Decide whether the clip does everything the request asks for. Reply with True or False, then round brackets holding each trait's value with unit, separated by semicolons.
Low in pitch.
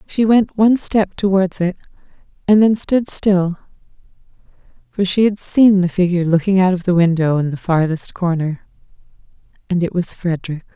False (185 Hz)